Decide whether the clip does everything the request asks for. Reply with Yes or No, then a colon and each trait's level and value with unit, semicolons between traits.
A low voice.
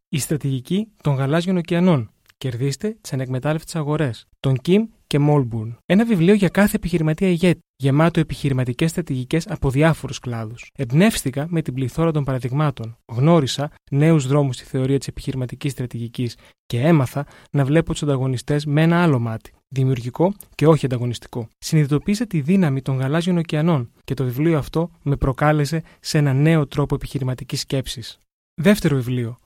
No: medium, 145 Hz